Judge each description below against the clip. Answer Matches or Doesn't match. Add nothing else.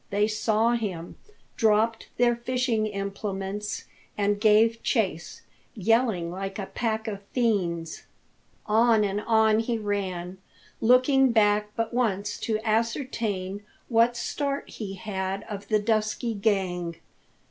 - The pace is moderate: Doesn't match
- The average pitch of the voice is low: Doesn't match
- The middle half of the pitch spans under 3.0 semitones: Matches